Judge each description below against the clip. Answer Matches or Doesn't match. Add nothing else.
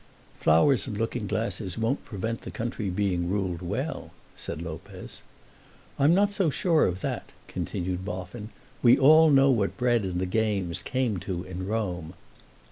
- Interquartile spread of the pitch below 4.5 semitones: Doesn't match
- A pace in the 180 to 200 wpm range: Doesn't match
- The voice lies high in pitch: Doesn't match